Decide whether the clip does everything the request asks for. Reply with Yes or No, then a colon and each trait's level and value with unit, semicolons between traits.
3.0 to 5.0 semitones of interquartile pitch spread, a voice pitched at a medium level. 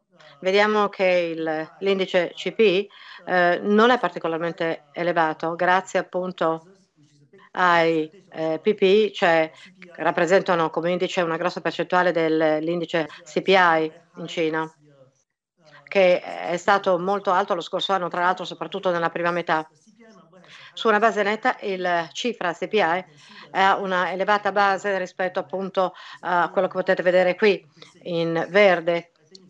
No: narrow, 2.6 semitones; medium, 180 Hz